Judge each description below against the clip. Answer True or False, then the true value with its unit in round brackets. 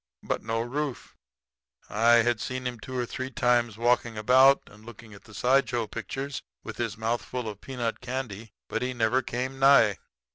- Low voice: True (120 Hz)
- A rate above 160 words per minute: True (180 wpm)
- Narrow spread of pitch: True (2.3 semitones)